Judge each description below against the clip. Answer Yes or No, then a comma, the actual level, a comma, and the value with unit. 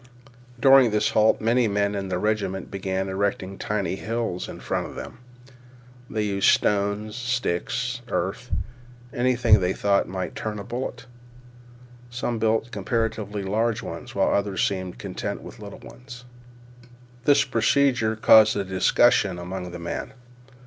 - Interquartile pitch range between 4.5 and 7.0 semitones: No, average, 3.7 semitones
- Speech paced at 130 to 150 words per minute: Yes, average, 140 wpm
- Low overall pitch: Yes, low, 105 Hz